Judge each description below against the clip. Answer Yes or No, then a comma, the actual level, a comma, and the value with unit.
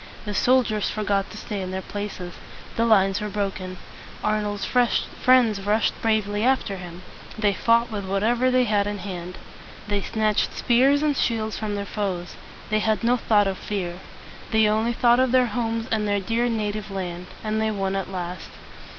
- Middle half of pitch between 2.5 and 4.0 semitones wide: Yes, average, 2.8 semitones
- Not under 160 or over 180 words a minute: Yes, average, 175 wpm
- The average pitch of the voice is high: Yes, high, 210 Hz